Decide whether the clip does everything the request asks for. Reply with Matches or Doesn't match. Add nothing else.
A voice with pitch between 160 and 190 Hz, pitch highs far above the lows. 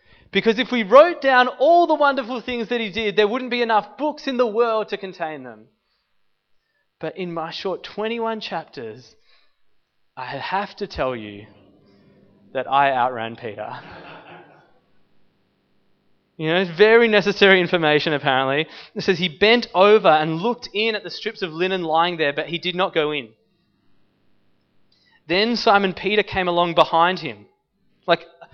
Matches